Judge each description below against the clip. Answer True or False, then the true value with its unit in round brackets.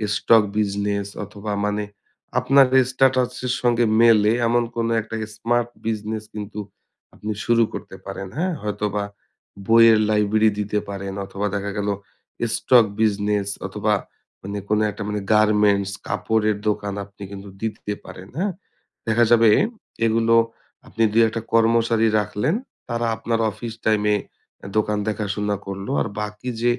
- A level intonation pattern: True (2.0 semitones)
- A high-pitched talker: False (105 Hz)